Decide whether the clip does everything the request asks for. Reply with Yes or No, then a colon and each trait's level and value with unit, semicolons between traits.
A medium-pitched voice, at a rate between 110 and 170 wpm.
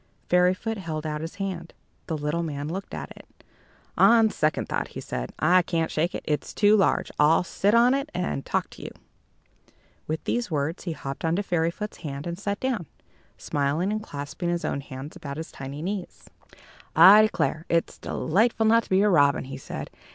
No: medium, 170 Hz; average, 190 wpm